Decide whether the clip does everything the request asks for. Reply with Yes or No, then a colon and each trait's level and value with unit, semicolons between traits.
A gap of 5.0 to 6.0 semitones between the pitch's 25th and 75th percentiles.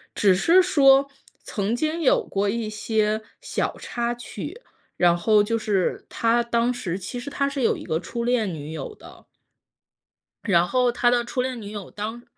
No: average, 3.5 semitones